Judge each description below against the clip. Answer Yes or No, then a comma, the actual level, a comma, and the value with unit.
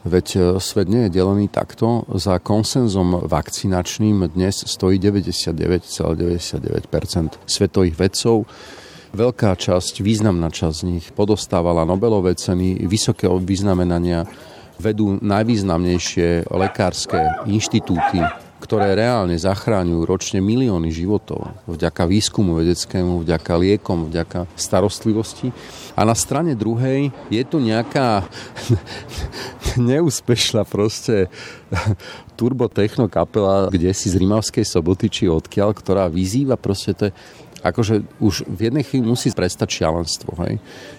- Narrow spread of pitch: No, average, 3.9 semitones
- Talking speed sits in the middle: No, slow, 105 wpm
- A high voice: No, low, 100 Hz